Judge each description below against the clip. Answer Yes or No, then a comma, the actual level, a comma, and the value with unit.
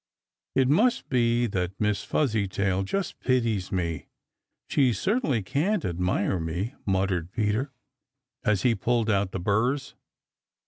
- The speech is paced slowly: Yes, slow, 125 wpm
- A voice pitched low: Yes, low, 105 Hz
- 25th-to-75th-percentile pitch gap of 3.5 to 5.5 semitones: Yes, average, 5.1 semitones